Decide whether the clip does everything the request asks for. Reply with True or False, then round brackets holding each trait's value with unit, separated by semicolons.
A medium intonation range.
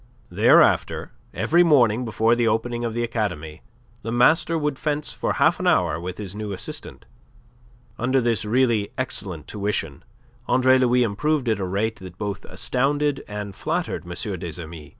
True (4.7 semitones)